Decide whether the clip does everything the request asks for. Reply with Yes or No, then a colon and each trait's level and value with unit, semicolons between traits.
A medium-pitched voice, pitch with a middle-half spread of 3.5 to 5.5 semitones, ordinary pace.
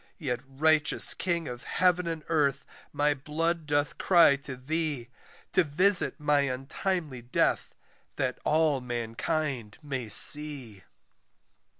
No: medium, 145 Hz; average, 3.8 semitones; slow, 115 wpm